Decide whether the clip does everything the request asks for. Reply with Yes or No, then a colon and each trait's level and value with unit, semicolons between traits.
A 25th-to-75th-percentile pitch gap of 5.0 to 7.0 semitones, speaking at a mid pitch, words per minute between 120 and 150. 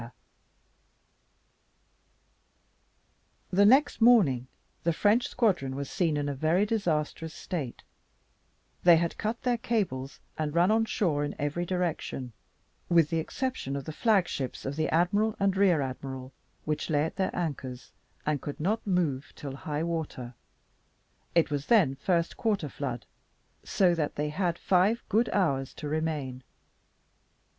Yes: wide, 5.4 semitones; medium, 165 Hz; average, 140 wpm